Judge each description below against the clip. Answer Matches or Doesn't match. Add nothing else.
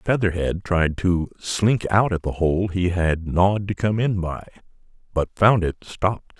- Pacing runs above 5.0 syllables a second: Doesn't match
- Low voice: Matches